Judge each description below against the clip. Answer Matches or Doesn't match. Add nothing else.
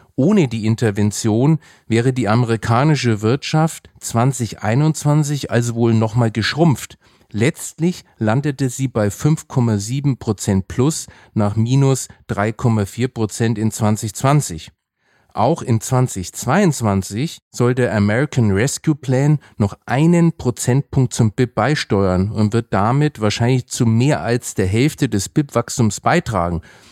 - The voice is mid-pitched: Doesn't match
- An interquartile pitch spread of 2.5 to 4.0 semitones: Doesn't match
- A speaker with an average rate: Doesn't match